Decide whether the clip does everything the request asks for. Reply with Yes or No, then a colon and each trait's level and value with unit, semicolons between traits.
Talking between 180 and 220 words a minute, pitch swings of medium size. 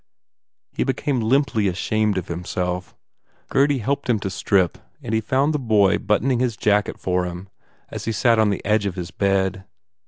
Yes: average, 185 wpm; average, 4.5 semitones